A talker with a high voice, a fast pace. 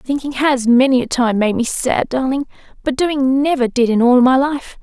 Yes: very high, 260 Hz; fast, 210 wpm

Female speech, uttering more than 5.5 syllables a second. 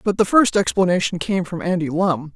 No: female; 5.3 syllables/s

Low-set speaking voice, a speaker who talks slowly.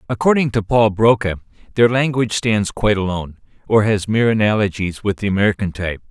No: low, 105 Hz; average, 165 wpm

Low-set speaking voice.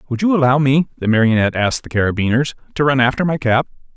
Yes: low, 130 Hz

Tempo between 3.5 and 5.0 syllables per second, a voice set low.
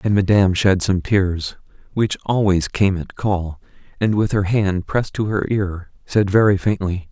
Yes: 4.5 syllables/s; very low, 95 Hz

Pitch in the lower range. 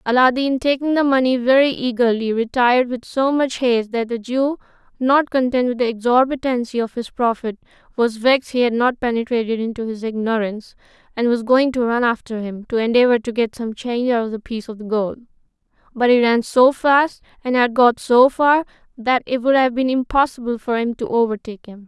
No: high, 245 Hz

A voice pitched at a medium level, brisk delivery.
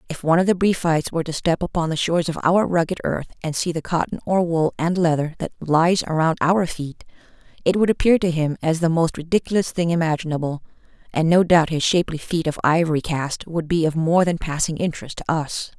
Yes: medium, 165 Hz; fast, 215 wpm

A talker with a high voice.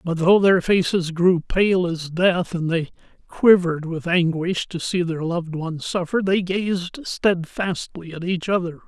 No: medium, 175 Hz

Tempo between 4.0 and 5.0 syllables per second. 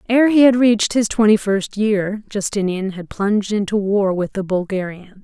Yes: 4.8 syllables/s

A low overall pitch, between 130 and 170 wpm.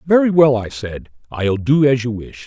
No: low, 130 Hz; fast, 220 wpm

